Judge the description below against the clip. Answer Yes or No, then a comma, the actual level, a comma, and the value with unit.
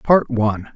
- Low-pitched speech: Yes, low, 125 Hz